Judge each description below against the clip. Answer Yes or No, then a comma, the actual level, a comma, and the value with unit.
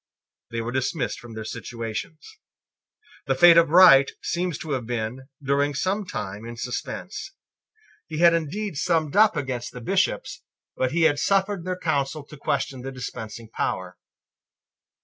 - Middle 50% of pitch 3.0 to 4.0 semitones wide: No, wide, 5.5 semitones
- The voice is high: No, medium, 140 Hz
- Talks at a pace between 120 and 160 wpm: Yes, average, 150 wpm